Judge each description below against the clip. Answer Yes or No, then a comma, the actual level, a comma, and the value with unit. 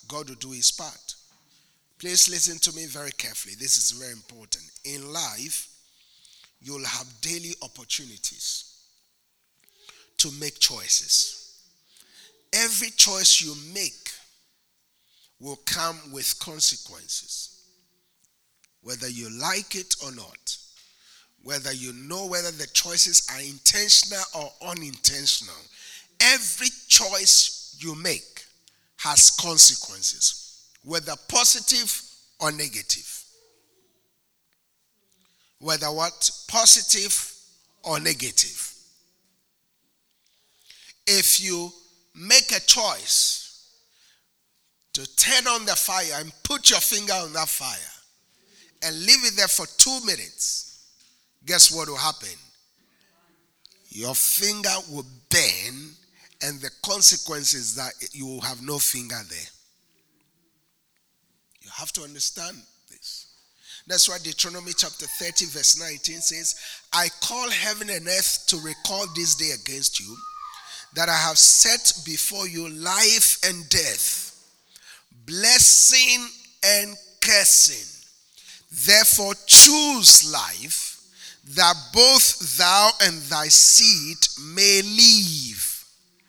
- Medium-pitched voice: Yes, medium, 170 Hz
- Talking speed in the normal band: No, slow, 105 wpm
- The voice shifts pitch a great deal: Yes, wide, 5.8 semitones